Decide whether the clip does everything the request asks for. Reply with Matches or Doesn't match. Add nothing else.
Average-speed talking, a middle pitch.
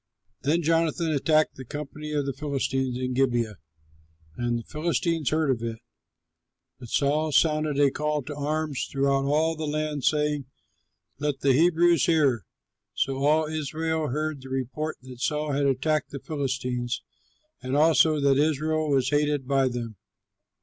Matches